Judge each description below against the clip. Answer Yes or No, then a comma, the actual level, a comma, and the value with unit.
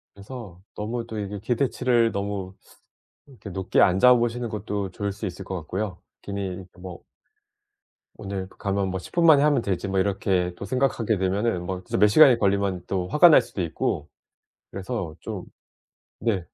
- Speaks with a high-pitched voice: No, low, 100 Hz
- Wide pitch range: No, average, 3.7 semitones